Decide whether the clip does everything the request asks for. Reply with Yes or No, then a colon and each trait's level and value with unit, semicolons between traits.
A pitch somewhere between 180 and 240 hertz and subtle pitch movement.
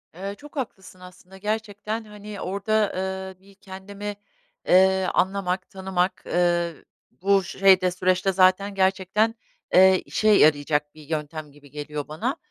Yes: high, 190 Hz; narrow, 1.9 semitones